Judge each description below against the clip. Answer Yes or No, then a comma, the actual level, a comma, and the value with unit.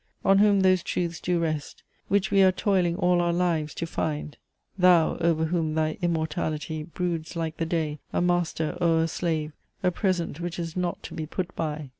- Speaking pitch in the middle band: Yes, medium, 170 Hz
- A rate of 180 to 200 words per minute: Yes, average, 190 wpm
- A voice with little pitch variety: Yes, narrow, 2.2 semitones